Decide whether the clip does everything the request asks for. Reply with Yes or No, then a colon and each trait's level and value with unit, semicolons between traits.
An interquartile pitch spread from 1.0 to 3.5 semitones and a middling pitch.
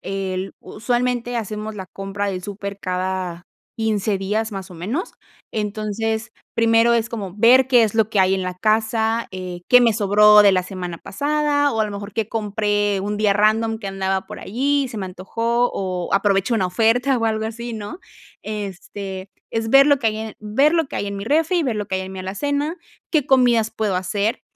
No: average, 3.0 semitones; high, 215 Hz